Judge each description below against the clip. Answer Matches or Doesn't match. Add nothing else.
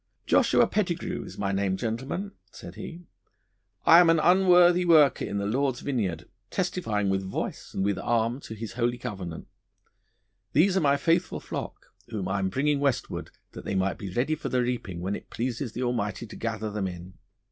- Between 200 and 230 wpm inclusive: Doesn't match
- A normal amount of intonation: Doesn't match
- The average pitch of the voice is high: Doesn't match